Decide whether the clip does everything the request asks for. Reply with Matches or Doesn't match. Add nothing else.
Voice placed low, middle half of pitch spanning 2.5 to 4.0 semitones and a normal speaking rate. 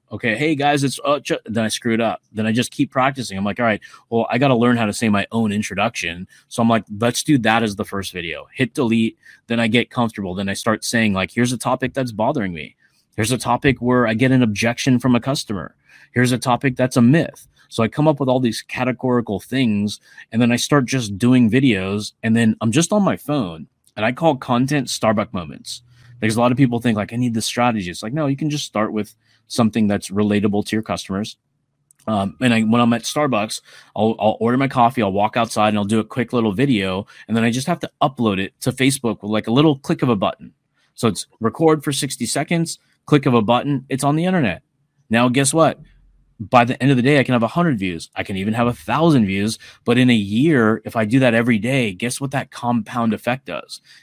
Doesn't match